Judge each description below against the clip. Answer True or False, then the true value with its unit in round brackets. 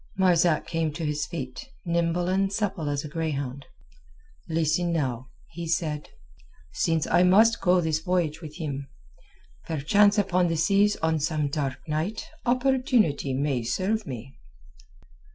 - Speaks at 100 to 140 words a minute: True (135 wpm)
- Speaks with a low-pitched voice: False (165 Hz)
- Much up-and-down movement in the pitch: False (3.7 semitones)